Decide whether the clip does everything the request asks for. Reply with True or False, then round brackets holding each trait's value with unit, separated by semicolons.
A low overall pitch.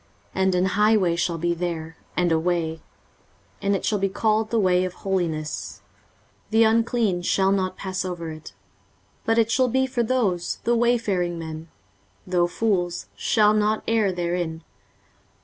False (185 Hz)